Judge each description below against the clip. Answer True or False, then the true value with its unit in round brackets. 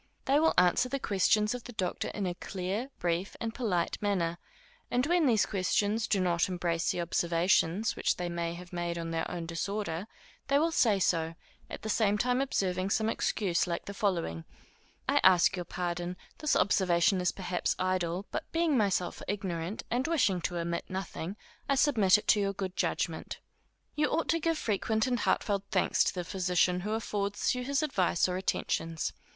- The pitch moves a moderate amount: True (4.1 semitones)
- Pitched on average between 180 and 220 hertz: True (190 Hz)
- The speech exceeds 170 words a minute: True (185 wpm)